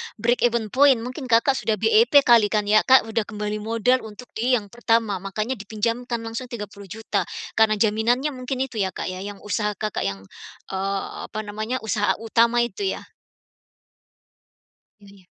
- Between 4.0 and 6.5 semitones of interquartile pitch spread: No, average, 2.9 semitones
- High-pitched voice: Yes, high, 225 Hz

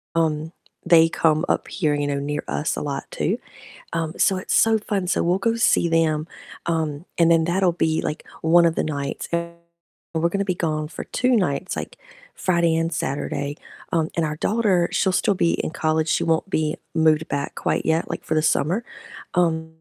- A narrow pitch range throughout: Yes, narrow, 2.2 semitones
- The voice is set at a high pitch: No, medium, 165 Hz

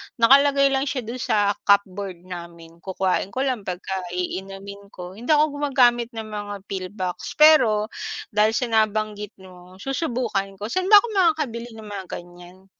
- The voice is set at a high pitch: Yes, high, 210 Hz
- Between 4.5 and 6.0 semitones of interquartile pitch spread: Yes, average, 5.1 semitones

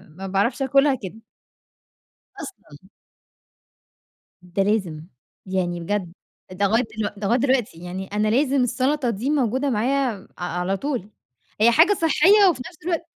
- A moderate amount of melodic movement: No, wide, 6.3 semitones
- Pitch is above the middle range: Yes, high, 225 Hz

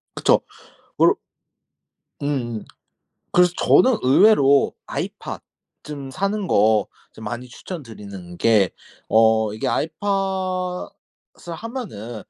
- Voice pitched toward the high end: No, medium, 140 Hz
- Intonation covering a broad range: Yes, wide, 9.0 semitones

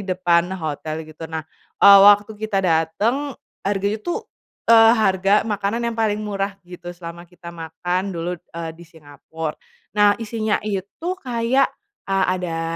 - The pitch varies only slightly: No, average, 4.0 semitones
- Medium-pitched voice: No, high, 195 Hz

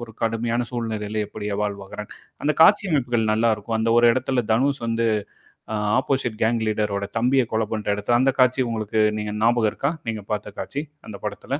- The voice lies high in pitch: No, low, 115 Hz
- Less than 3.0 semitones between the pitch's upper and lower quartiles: Yes, narrow, 2.4 semitones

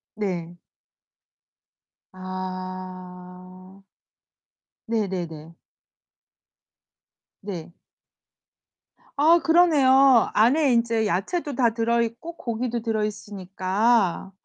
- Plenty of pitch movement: No, average, 4.4 semitones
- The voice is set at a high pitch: Yes, high, 210 Hz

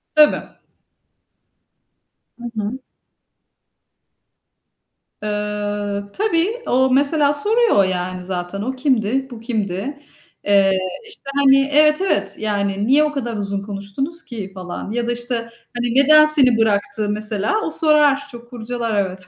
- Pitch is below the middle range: No, high, 235 Hz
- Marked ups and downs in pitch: Yes, wide, 5.9 semitones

